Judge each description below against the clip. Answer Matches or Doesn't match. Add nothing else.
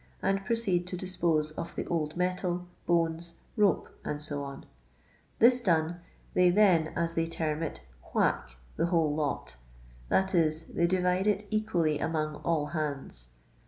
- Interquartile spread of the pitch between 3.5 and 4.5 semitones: Doesn't match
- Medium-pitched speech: Matches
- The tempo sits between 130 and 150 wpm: Matches